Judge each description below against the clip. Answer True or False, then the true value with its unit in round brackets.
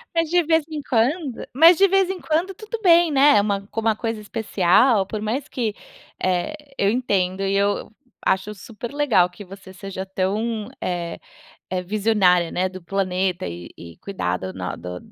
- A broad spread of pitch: True (6.7 semitones)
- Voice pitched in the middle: False (205 Hz)